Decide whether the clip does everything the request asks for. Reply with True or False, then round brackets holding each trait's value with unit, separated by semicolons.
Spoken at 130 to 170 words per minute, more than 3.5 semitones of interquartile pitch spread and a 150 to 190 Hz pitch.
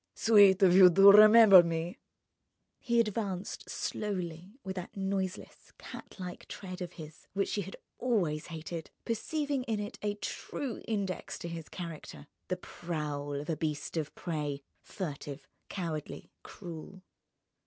True (140 wpm; 4.0 semitones; 185 Hz)